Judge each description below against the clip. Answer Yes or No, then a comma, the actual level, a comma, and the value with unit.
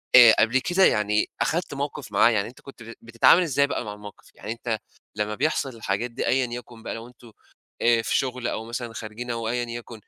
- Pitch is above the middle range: No, low, 120 Hz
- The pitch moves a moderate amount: No, narrow, 2.2 semitones